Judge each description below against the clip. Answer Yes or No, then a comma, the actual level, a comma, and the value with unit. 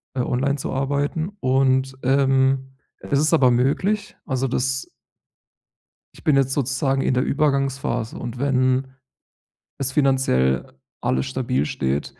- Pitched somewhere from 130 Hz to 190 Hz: Yes, low, 135 Hz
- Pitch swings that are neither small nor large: No, narrow, 1.4 semitones